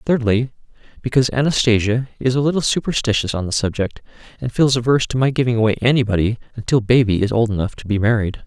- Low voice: Yes, low, 120 Hz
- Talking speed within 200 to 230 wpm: No, average, 185 wpm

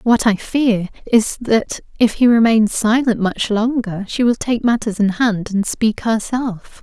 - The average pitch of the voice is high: Yes, high, 220 Hz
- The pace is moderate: Yes, average, 175 wpm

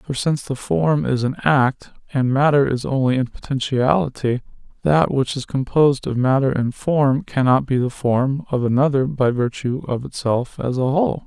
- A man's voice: Yes, male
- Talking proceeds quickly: No, average, 180 wpm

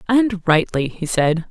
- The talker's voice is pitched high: No, medium, 180 Hz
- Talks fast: No, average, 160 wpm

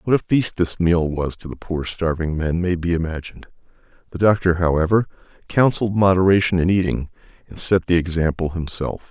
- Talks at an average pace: Yes, average, 170 wpm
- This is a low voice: Yes, very low, 90 Hz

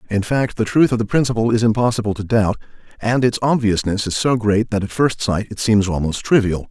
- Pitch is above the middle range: No, low, 110 Hz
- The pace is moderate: No, fast, 225 wpm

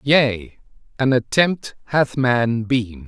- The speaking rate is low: Yes, slow, 115 wpm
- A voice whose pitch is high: No, low, 120 Hz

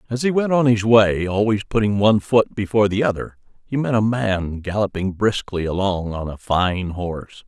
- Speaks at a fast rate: No, average, 195 wpm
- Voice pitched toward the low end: Yes, low, 105 Hz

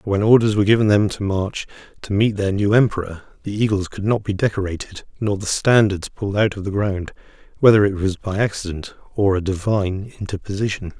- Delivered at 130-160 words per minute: No, average, 195 wpm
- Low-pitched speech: Yes, low, 100 Hz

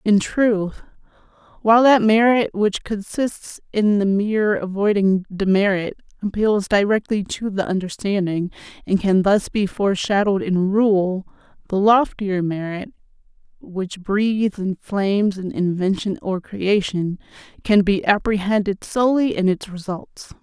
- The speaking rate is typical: No, slow, 125 wpm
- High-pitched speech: Yes, high, 200 Hz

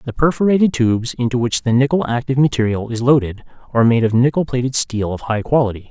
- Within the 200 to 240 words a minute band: Yes, fast, 205 wpm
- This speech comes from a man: Yes, male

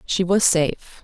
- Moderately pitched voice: Yes, medium, 175 Hz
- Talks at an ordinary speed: Yes, average, 175 wpm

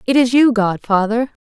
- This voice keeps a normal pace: Yes, average, 170 wpm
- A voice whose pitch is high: Yes, high, 235 Hz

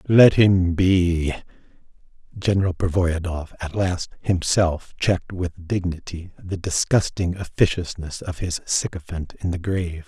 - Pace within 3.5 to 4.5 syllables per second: Yes, 4.3 syllables/s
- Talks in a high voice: No, very low, 90 Hz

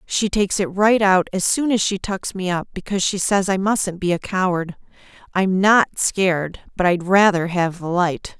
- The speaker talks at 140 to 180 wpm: No, fast, 205 wpm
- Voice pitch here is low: No, high, 190 Hz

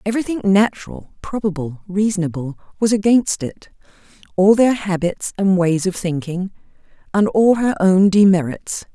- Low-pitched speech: No, high, 195 Hz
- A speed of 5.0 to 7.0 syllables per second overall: No, 4.8 syllables/s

